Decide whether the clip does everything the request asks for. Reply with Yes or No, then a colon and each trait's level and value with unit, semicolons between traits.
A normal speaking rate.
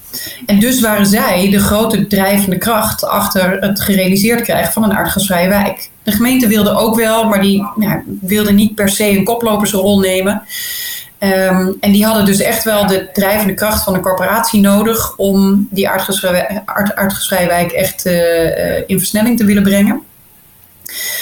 Yes: average, 165 wpm